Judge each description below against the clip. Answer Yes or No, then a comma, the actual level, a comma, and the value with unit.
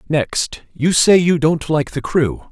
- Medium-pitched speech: Yes, medium, 155 Hz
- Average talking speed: Yes, average, 190 wpm